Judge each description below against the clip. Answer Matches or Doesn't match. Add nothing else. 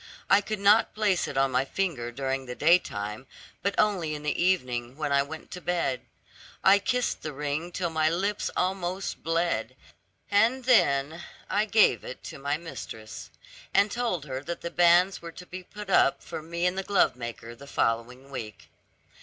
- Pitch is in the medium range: Matches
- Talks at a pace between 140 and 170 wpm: Doesn't match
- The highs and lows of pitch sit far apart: Matches